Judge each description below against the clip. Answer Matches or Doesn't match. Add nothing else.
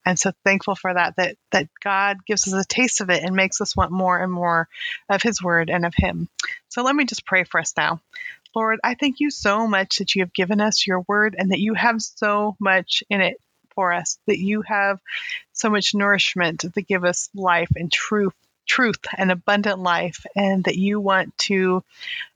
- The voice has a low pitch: Doesn't match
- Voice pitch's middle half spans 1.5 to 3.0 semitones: Matches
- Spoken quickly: Matches